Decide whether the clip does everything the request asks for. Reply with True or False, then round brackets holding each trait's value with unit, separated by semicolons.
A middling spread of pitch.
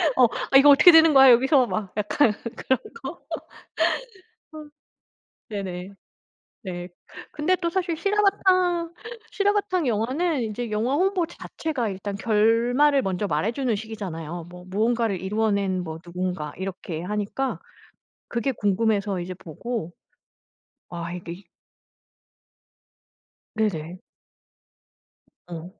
False (7.1 semitones)